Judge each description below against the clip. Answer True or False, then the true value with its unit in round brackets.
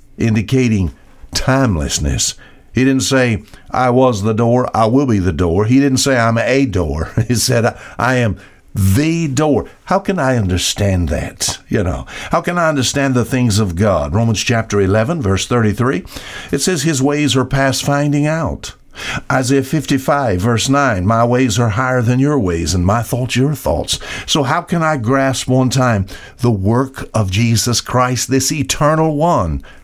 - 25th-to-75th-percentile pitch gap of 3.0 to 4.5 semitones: True (4.2 semitones)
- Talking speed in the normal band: True (175 wpm)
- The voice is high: False (125 Hz)